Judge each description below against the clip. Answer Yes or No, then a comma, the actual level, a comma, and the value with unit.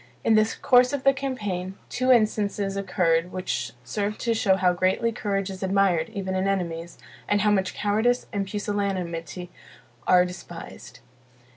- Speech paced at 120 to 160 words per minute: Yes, average, 150 wpm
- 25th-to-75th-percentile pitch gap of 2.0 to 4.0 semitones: Yes, average, 2.8 semitones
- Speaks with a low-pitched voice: No, high, 195 Hz